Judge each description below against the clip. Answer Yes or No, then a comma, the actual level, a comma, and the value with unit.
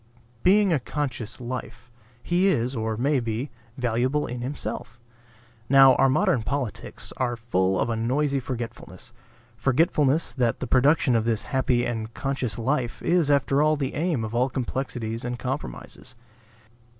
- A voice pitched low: Yes, low, 125 Hz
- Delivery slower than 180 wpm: Yes, average, 150 wpm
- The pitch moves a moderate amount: Yes, average, 3.4 semitones